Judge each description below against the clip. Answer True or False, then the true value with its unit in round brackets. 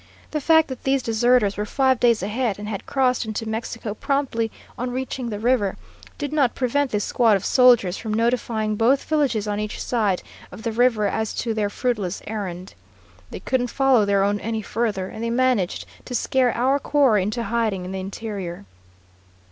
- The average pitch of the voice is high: True (230 Hz)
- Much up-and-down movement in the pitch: False (3.4 semitones)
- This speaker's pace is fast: False (185 wpm)